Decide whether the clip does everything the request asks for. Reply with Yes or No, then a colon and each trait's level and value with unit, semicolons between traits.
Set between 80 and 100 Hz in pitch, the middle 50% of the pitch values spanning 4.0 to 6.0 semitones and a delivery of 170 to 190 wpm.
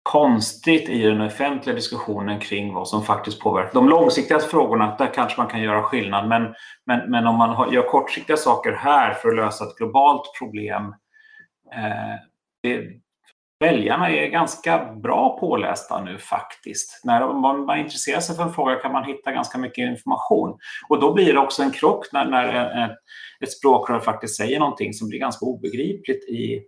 No: low, 120 Hz; average, 4.3 semitones; average, 175 wpm